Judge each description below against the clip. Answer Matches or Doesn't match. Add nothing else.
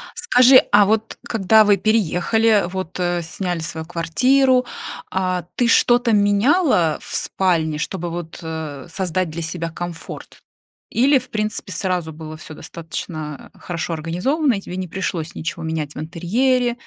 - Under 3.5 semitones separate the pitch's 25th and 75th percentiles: Doesn't match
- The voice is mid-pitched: Matches